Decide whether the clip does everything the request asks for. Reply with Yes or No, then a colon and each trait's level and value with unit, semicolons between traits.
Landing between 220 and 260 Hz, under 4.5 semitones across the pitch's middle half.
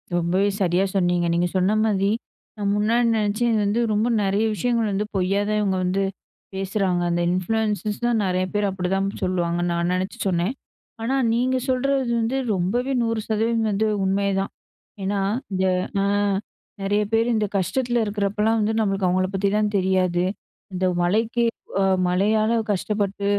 No: high, 200 Hz; average, 2.9 semitones